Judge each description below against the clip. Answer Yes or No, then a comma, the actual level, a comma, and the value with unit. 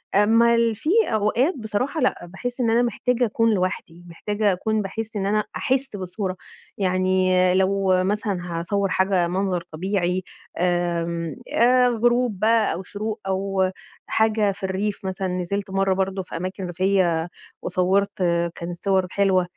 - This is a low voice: No, high, 195 Hz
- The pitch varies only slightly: No, average, 3.0 semitones